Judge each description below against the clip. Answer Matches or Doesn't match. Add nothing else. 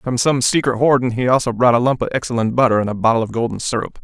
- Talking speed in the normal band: Doesn't match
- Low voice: Matches